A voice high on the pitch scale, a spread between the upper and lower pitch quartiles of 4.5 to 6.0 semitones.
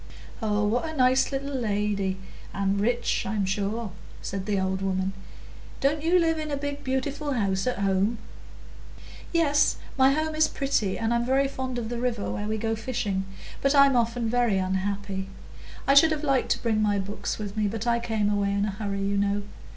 Yes: high, 225 Hz; average, 5.0 semitones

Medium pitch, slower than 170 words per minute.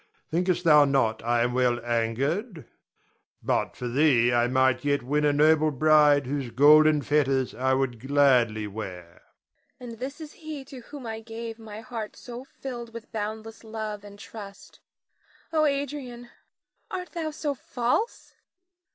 Yes: medium, 155 Hz; average, 150 wpm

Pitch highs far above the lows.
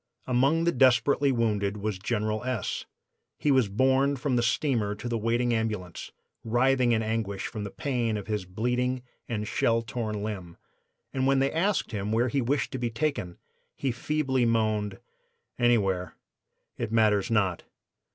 No: average, 3.5 semitones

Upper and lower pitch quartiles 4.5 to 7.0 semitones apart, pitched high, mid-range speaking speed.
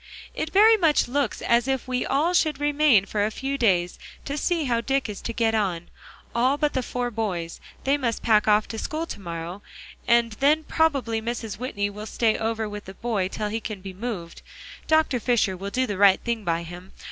No: average, 5.0 semitones; high, 230 Hz; fast, 210 wpm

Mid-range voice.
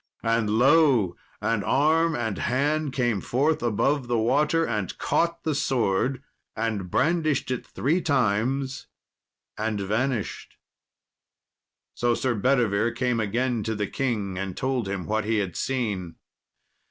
No: low, 120 Hz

